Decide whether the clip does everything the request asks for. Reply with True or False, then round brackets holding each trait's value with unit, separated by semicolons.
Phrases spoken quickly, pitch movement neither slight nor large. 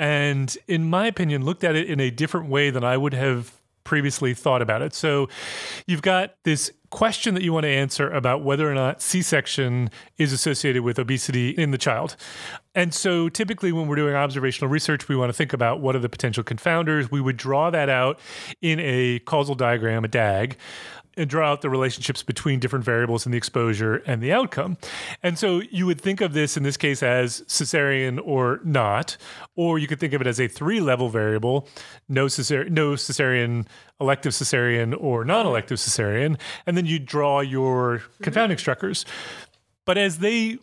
False (190 wpm; 4.2 semitones)